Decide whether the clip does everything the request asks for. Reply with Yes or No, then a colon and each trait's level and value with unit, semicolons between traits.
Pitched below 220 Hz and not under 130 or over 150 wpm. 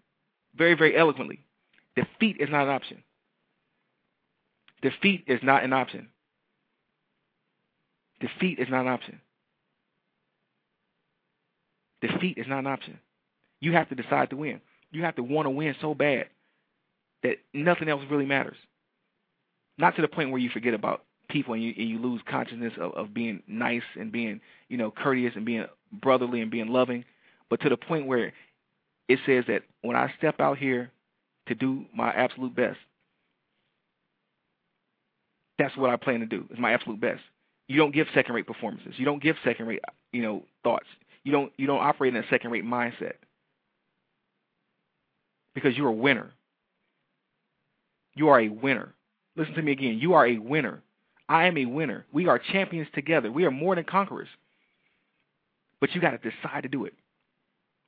No: low, 135 Hz; average, 165 wpm